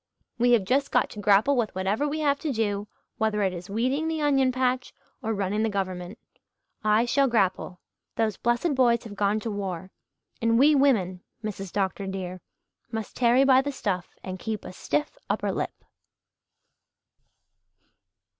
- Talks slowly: No, average, 165 wpm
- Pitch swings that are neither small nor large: Yes, average, 4.8 semitones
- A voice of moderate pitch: No, high, 220 Hz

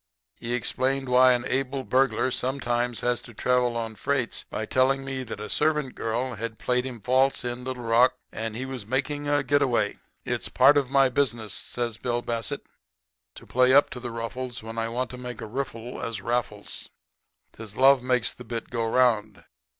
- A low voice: Yes, low, 125 Hz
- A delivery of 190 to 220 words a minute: Yes, average, 195 wpm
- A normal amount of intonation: No, narrow, 2.2 semitones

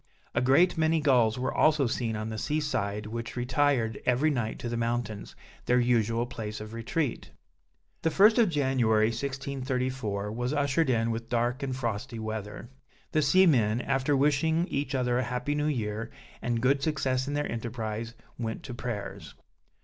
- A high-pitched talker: No, low, 125 Hz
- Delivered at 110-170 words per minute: Yes, average, 165 wpm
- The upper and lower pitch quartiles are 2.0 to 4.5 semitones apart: Yes, average, 3.7 semitones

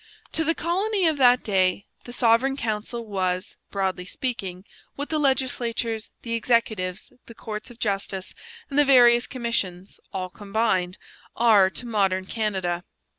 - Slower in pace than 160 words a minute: Yes, average, 140 wpm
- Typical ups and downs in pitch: Yes, average, 4.5 semitones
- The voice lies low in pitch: No, high, 225 Hz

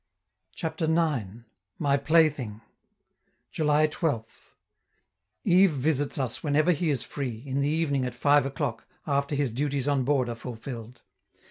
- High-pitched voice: No, medium, 140 Hz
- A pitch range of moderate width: Yes, average, 3.5 semitones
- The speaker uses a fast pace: No, slow, 135 wpm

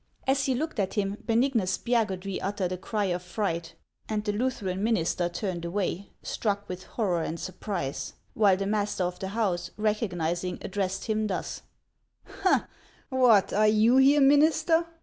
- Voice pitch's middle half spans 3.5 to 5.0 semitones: Yes, average, 3.8 semitones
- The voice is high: Yes, high, 205 Hz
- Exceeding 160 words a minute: No, average, 155 wpm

